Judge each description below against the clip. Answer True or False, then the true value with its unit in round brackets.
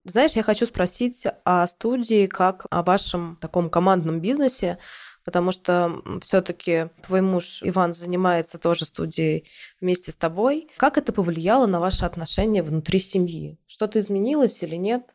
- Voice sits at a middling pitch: True (180 Hz)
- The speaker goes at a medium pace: True (145 wpm)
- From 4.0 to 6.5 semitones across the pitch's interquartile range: False (3.4 semitones)